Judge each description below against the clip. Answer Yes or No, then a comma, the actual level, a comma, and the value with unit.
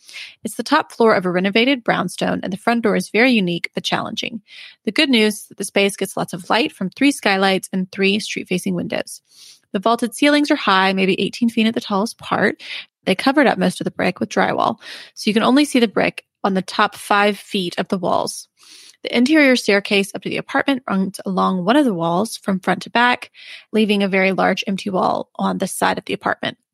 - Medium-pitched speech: No, high, 210 Hz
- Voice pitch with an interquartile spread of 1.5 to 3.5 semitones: No, average, 4.0 semitones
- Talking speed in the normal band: No, fast, 225 wpm